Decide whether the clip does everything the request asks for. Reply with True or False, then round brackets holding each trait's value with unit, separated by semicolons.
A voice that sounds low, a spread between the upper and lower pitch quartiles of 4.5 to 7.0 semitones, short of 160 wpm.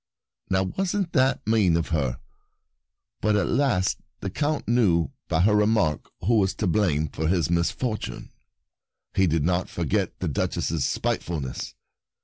True (95 Hz; 5.2 semitones; 145 wpm)